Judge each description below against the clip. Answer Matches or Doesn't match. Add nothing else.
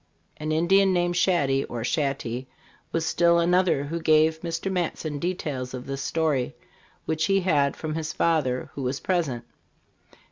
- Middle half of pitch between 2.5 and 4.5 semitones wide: Matches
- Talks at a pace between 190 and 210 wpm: Doesn't match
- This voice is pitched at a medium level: Matches